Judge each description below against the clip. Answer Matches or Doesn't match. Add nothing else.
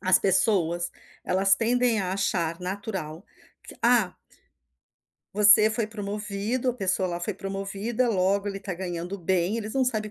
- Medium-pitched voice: Doesn't match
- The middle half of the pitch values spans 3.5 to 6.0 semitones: Doesn't match